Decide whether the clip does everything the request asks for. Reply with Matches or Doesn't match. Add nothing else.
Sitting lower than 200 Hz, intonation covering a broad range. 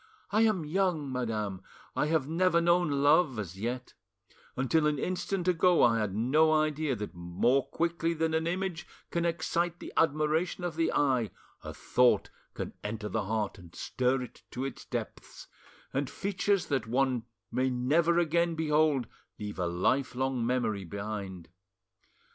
Matches